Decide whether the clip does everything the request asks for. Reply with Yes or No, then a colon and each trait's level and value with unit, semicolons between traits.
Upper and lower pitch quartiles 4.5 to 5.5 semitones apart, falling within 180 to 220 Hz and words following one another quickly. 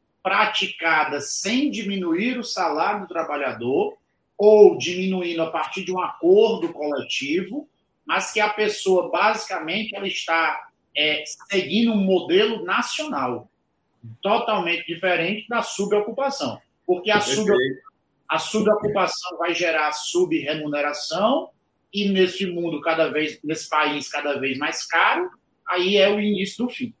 No: average, 4.9 semitones; high, 190 Hz; average, 125 wpm